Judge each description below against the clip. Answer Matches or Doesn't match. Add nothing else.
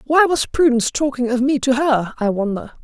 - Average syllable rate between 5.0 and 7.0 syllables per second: Matches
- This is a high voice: Matches